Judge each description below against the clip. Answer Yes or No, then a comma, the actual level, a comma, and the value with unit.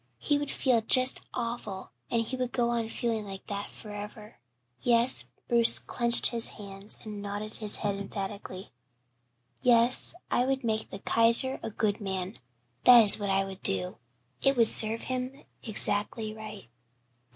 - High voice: Yes, high, 220 Hz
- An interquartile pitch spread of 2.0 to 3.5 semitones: Yes, average, 2.8 semitones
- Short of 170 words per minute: Yes, average, 155 wpm